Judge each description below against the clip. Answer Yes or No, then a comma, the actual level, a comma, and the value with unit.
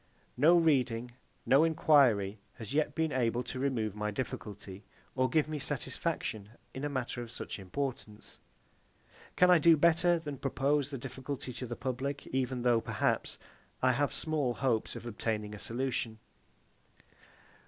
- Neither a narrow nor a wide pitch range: Yes, average, 4.1 semitones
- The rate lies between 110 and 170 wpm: Yes, average, 150 wpm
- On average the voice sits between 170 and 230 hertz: No, low, 130 Hz